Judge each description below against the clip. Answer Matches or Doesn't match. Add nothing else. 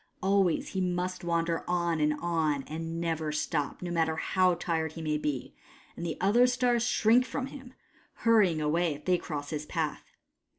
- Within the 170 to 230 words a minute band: Matches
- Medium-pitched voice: Matches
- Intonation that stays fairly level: Doesn't match